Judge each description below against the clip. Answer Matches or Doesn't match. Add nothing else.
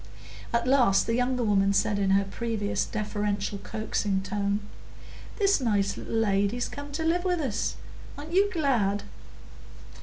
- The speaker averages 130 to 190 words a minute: Matches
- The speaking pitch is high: Matches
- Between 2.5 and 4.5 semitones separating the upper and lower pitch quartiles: Doesn't match